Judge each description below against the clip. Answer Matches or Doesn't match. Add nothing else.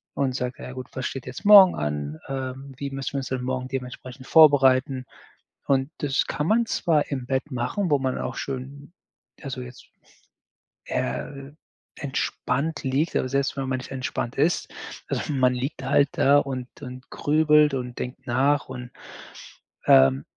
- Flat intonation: Matches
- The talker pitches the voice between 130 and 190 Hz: Matches